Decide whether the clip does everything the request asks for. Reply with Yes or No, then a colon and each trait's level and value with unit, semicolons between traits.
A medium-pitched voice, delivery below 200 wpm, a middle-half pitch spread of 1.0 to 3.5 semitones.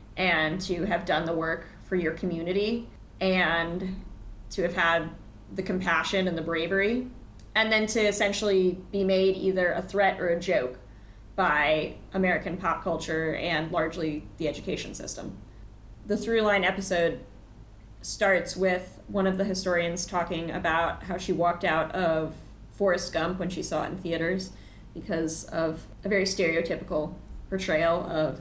Yes: medium, 175 Hz; average, 150 wpm; average, 2.8 semitones